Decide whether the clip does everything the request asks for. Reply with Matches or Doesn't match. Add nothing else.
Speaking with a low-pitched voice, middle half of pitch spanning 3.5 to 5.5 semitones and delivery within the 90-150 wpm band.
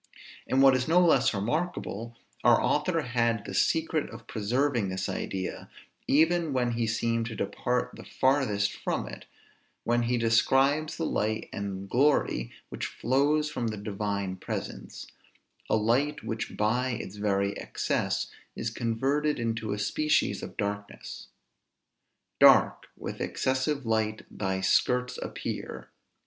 Matches